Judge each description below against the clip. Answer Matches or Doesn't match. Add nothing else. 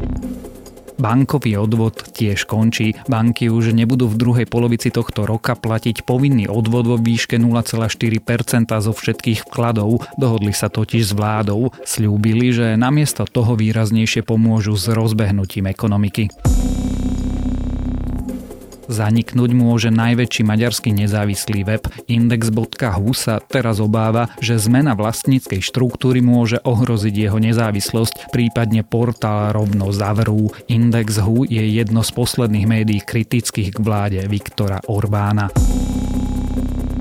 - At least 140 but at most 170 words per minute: Doesn't match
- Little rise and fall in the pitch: Matches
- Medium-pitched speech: Doesn't match